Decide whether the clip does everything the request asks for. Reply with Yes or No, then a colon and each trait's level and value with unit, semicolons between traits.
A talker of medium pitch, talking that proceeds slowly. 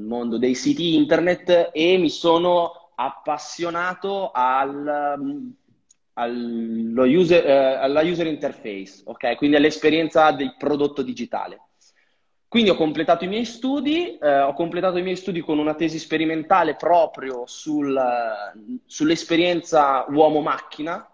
Yes: medium, 155 Hz; slow, 105 wpm